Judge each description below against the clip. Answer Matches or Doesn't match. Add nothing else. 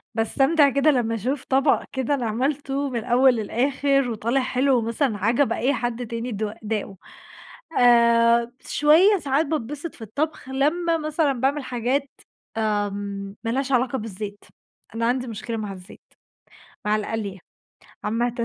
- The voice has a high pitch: Matches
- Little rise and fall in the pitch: Doesn't match